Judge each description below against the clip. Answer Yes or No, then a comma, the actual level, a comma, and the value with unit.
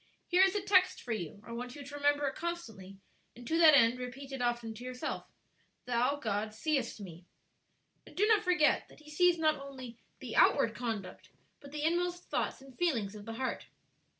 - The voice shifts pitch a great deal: Yes, wide, 5.7 semitones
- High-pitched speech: Yes, very high, 270 Hz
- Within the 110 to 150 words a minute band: No, average, 200 wpm